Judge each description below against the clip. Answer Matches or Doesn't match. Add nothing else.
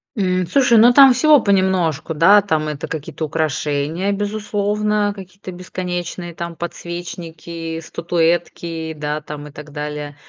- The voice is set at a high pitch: Doesn't match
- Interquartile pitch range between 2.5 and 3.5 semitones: Doesn't match